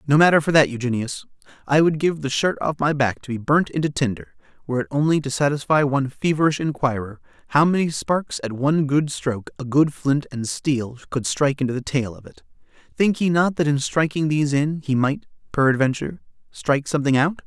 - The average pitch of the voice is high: No, medium, 140 Hz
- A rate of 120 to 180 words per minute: No, average, 200 wpm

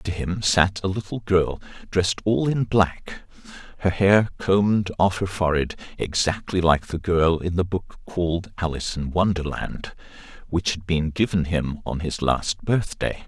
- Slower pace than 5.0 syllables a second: Yes, 4.6 syllables/s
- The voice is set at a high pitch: No, very low, 90 Hz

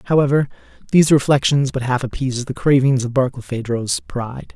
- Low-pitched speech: Yes, low, 130 Hz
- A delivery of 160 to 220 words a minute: No, average, 145 wpm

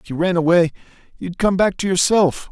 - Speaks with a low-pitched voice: No, medium, 180 Hz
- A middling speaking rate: No, fast, 215 wpm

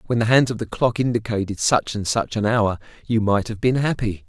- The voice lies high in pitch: No, low, 110 Hz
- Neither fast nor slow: No, fast, 240 wpm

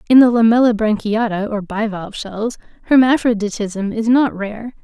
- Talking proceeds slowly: Yes, slow, 125 wpm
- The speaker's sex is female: Yes, female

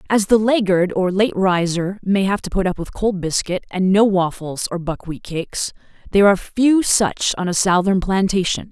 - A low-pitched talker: No, high, 190 Hz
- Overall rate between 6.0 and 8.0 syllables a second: No, 4.9 syllables/s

